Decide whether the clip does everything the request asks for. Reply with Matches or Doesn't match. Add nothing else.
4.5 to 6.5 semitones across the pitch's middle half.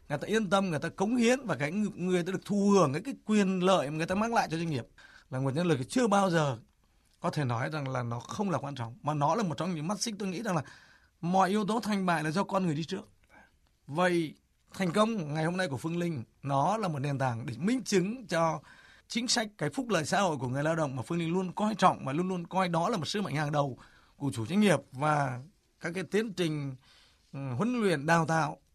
Matches